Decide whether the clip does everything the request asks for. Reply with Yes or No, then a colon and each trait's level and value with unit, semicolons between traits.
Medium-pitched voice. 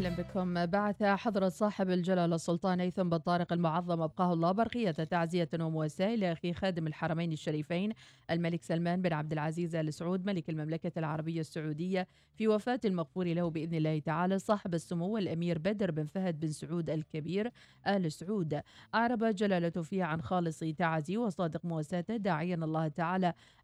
Yes: medium, 175 Hz